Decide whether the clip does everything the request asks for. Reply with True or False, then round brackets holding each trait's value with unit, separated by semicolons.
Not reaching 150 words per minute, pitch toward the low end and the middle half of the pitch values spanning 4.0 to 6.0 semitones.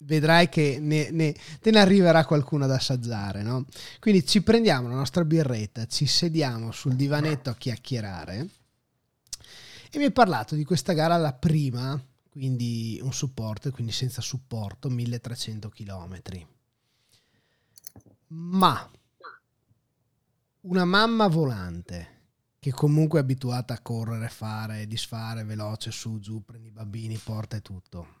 True (130 wpm; 125 Hz; 5.2 semitones)